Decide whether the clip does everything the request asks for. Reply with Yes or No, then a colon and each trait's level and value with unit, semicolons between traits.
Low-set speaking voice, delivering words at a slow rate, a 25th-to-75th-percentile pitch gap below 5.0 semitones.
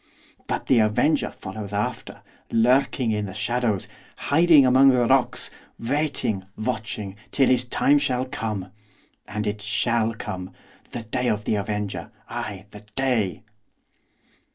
Yes: low, 115 Hz; slow, 130 wpm; average, 3.6 semitones